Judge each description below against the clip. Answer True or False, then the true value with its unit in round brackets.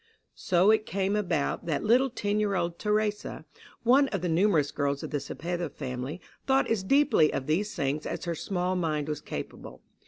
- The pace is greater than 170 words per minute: True (185 wpm)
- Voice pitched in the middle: True (180 Hz)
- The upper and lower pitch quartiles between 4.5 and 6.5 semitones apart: True (5.6 semitones)